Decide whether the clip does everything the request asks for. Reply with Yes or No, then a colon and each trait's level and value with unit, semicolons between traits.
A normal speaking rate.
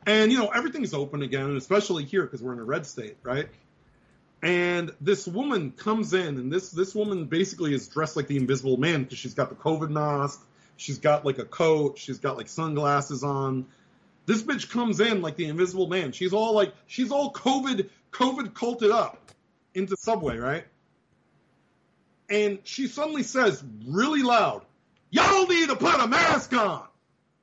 Yes: average, 175 wpm